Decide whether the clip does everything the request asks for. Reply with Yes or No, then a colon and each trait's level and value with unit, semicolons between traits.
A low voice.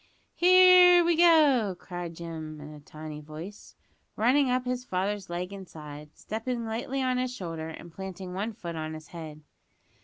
No: high, 190 Hz